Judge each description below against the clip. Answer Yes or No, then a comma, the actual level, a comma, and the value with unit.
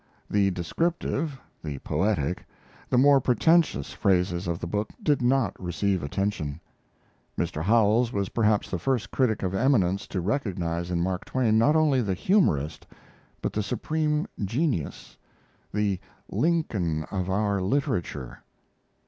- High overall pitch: No, low, 105 Hz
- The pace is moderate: No, slow, 130 wpm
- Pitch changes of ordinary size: No, wide, 6.7 semitones